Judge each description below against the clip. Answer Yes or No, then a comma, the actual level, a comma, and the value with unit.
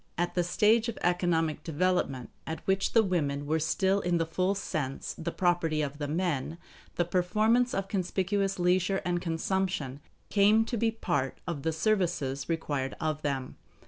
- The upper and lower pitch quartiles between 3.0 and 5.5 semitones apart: Yes, average, 3.9 semitones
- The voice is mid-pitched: Yes, medium, 175 Hz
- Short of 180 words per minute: Yes, average, 165 wpm